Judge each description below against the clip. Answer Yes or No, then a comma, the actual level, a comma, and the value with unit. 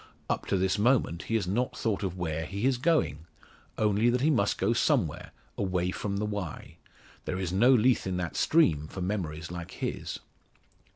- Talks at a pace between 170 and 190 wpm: Yes, average, 185 wpm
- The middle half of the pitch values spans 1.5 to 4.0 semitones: No, average, 4.6 semitones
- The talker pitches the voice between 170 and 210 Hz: No, low, 100 Hz